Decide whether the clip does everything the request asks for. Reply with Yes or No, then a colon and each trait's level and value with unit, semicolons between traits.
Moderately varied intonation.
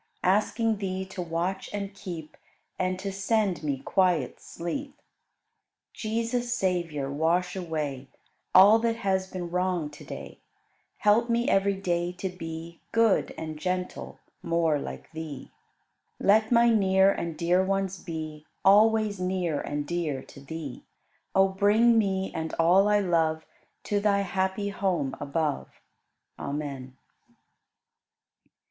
Yes: average, 3.8 semitones